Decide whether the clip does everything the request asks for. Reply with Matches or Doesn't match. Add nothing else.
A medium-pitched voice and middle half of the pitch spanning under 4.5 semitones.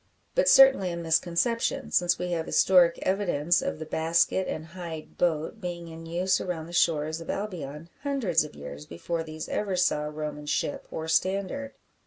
Matches